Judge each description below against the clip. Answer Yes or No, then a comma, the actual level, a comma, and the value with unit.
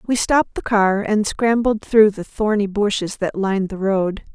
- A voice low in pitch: No, high, 205 Hz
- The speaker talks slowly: No, average, 195 wpm